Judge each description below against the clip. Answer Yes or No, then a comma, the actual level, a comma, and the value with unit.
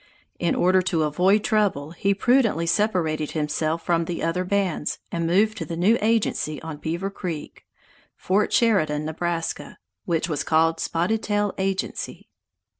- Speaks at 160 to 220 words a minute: No, average, 145 wpm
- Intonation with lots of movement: No, average, 3.8 semitones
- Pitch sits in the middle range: Yes, medium, 175 Hz